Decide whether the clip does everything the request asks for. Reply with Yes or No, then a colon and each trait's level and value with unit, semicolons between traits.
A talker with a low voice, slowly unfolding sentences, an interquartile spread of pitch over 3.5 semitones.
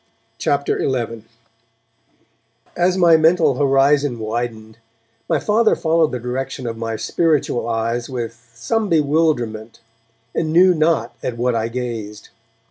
Yes: low, 125 Hz; slow, 125 wpm; wide, 5.6 semitones